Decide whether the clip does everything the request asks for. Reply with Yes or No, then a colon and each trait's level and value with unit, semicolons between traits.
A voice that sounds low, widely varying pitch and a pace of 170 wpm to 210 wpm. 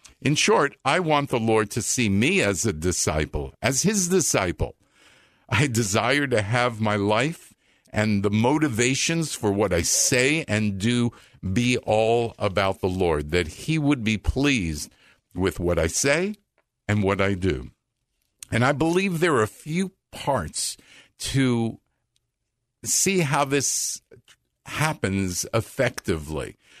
No: low, 120 Hz; wide, 5.8 semitones; average, 140 wpm